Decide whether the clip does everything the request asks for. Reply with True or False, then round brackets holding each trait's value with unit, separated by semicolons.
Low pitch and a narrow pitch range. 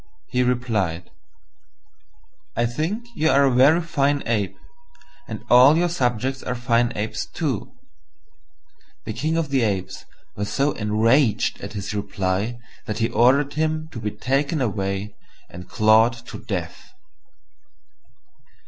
False (120 Hz; 5.1 semitones)